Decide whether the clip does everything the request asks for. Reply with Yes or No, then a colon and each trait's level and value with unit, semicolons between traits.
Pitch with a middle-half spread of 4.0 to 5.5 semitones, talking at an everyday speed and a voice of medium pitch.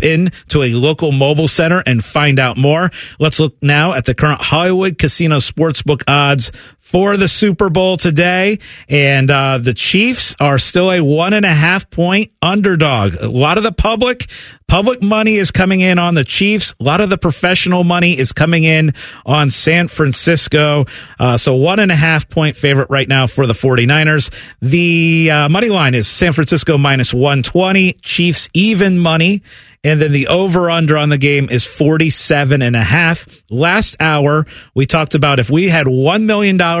Yes: average, 4.3 semitones; average, 185 wpm; medium, 155 Hz